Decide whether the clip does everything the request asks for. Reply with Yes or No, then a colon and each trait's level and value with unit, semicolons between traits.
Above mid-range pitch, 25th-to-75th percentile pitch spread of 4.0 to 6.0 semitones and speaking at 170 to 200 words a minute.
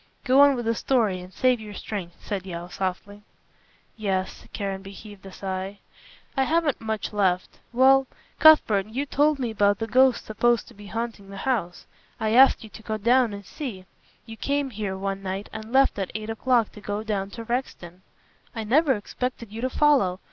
Yes: high, 220 Hz; average, 4.4 semitones; average, 190 wpm